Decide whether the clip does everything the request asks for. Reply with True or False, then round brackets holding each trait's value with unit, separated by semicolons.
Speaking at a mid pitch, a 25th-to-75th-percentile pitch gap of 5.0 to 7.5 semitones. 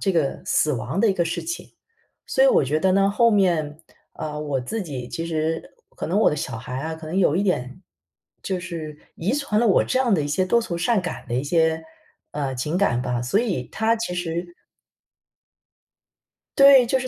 True (170 Hz; 5.5 semitones)